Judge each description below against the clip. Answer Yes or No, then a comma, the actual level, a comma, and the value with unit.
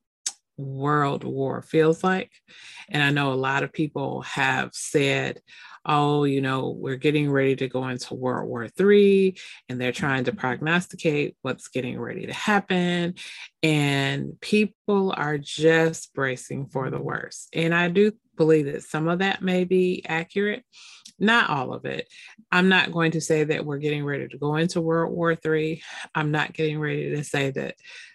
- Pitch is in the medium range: Yes, medium, 155 Hz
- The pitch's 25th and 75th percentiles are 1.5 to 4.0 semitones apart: No, average, 4.7 semitones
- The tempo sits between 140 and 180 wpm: Yes, average, 170 wpm